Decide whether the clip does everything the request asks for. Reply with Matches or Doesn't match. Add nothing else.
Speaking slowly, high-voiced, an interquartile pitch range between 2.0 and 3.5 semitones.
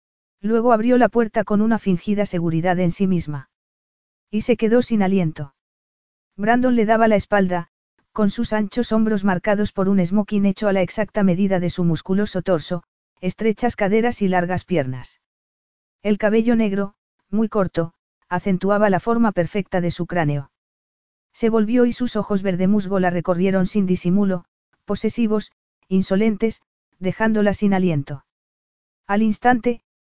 Doesn't match